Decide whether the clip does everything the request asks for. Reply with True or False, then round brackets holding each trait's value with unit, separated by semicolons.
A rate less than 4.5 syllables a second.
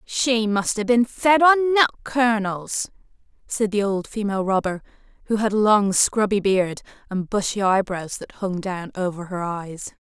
True (4.3 syllables/s)